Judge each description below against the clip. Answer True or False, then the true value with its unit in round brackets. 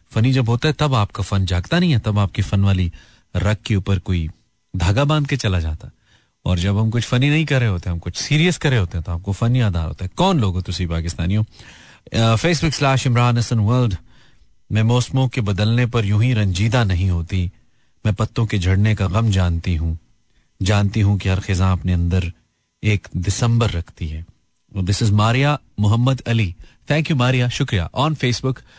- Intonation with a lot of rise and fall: False (4.9 semitones)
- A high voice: False (105 Hz)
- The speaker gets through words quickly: True (195 wpm)